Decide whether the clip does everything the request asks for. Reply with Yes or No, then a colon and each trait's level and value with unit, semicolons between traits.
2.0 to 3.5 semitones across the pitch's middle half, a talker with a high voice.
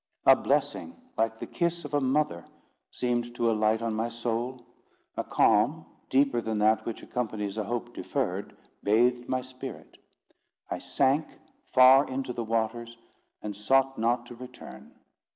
No: narrow, 2.5 semitones; low, 120 Hz